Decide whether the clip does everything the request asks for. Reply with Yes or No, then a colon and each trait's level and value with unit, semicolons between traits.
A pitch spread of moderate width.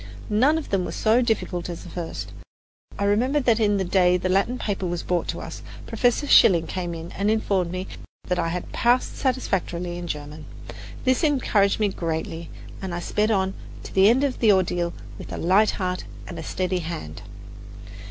Yes: average, 4.0 semitones